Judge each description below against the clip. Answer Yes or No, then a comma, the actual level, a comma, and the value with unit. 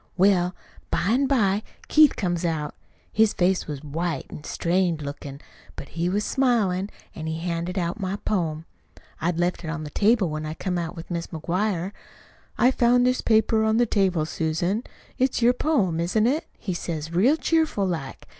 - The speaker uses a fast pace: No, average, 180 wpm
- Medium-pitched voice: Yes, medium, 180 Hz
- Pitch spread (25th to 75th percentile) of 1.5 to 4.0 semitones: No, average, 4.8 semitones